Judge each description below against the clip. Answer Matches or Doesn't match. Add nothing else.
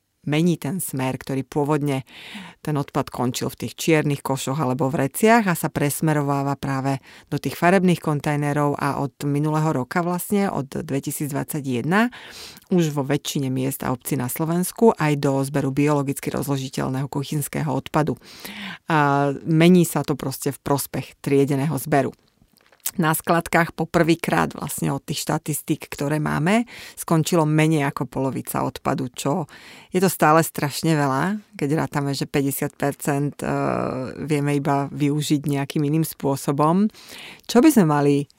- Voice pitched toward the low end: Doesn't match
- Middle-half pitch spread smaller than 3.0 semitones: Matches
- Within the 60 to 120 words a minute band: Doesn't match